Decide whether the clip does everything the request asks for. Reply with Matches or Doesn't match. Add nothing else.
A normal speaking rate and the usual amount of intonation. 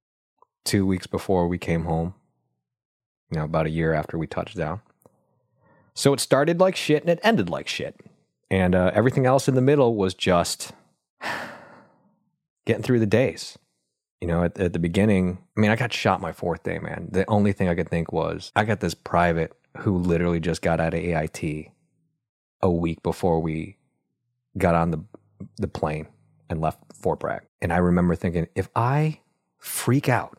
Doesn't match